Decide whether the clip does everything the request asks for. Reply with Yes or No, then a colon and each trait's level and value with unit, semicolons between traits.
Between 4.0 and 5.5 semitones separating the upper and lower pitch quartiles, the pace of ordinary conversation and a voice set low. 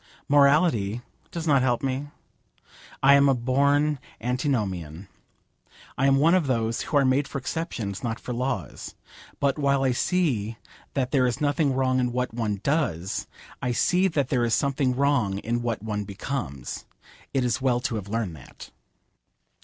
No: average, 3.6 semitones; average, 165 wpm; low, 130 Hz